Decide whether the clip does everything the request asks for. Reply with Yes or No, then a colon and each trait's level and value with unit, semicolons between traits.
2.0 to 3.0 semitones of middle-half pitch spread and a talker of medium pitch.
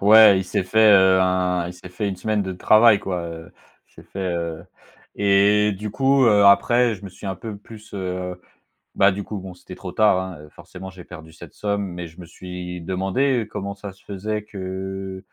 No: narrow, 2.4 semitones; very low, 95 Hz